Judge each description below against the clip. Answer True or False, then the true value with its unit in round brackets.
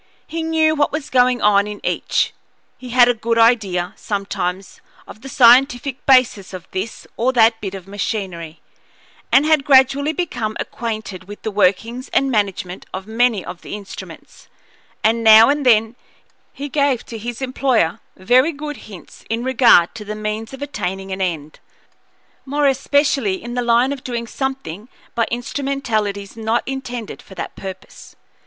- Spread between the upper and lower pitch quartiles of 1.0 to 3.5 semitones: False (4.7 semitones)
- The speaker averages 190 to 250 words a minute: False (160 wpm)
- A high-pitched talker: True (230 Hz)